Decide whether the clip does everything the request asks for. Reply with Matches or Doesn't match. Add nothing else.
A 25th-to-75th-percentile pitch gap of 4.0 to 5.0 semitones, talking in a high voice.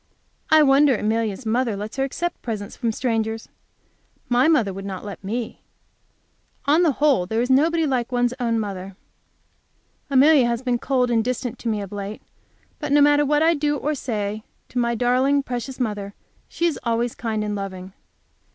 Matches